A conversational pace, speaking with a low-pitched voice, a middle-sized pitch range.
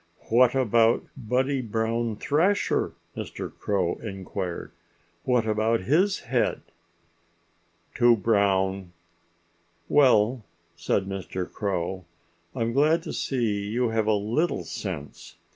No: slow, 110 wpm; low, 110 Hz; average, 4.2 semitones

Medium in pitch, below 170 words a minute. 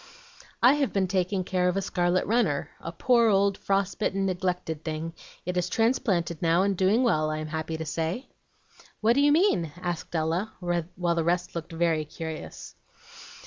No: medium, 180 Hz; average, 175 wpm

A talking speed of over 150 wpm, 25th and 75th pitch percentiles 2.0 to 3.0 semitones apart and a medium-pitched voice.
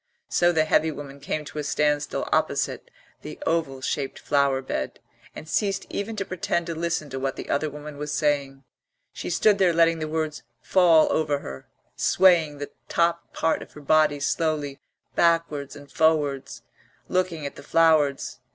Yes: average, 170 wpm; average, 2.7 semitones; medium, 155 Hz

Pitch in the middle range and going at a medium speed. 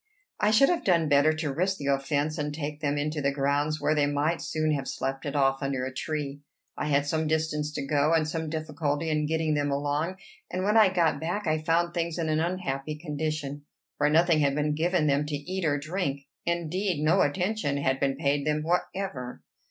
No: medium, 150 Hz; fast, 210 wpm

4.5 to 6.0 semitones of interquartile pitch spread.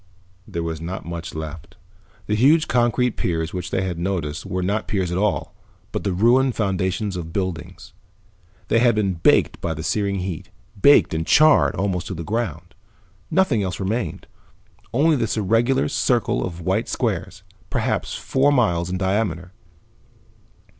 Yes: average, 4.9 semitones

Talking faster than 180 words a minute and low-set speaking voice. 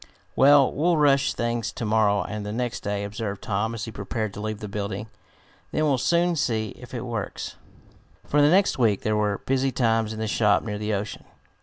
Yes: fast, 205 wpm; low, 110 Hz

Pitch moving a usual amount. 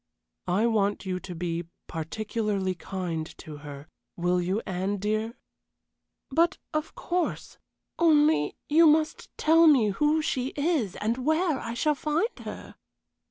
No: wide, 8.9 semitones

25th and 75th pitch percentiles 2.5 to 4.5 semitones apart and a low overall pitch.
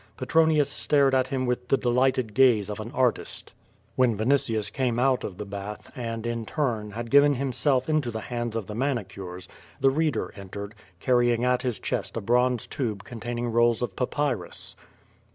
Yes: average, 3.2 semitones; low, 120 Hz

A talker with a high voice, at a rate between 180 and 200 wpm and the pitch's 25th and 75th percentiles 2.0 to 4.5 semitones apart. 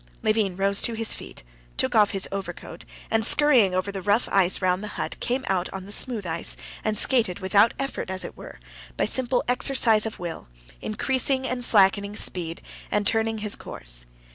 Yes: high, 210 Hz; average, 185 wpm; average, 3.8 semitones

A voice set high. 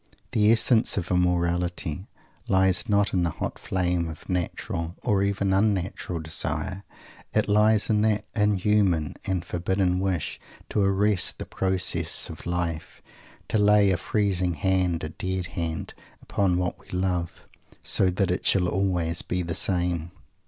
No: very low, 95 Hz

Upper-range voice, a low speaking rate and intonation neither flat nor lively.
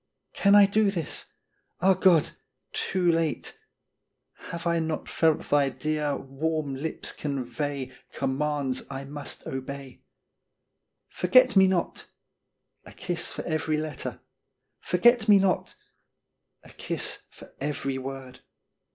No: medium, 155 Hz; slow, 130 wpm; average, 4.5 semitones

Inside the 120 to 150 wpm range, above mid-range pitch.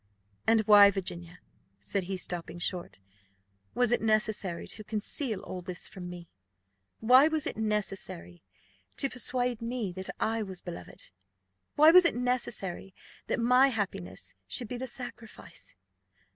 Yes: average, 140 wpm; high, 215 Hz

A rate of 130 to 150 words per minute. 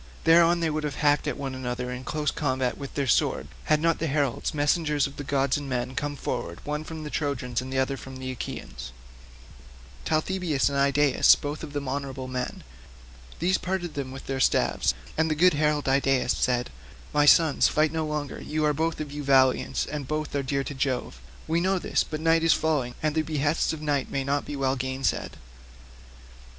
No: average, 200 wpm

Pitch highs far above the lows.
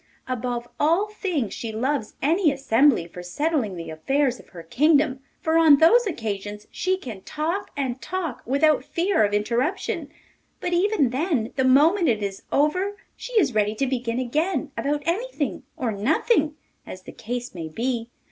Yes: wide, 6.3 semitones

